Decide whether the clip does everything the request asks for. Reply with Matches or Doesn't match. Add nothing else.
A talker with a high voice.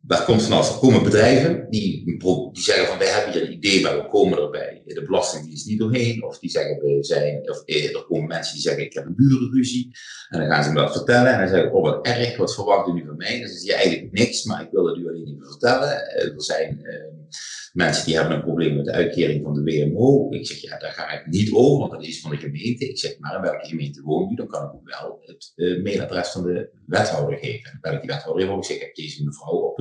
Doesn't match